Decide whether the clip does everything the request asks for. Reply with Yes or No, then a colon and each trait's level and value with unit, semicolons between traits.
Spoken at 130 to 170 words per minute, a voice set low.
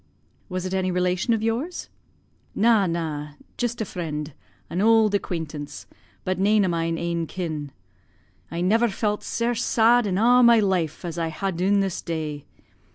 No: average, 160 wpm; medium, 185 Hz